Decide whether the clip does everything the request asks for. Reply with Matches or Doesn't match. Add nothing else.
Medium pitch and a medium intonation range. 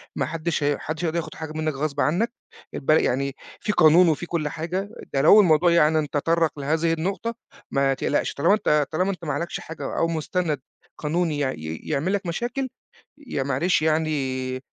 Matches